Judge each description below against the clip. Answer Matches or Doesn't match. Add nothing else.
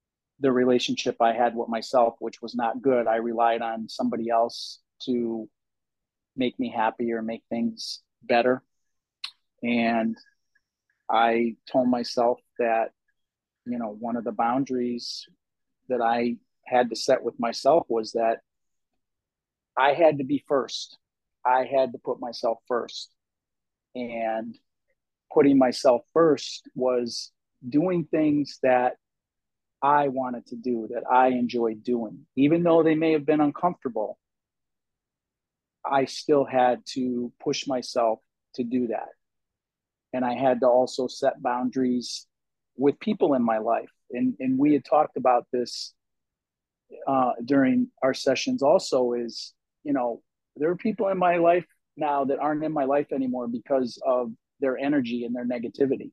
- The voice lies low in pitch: Matches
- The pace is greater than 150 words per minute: Doesn't match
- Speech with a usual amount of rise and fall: Matches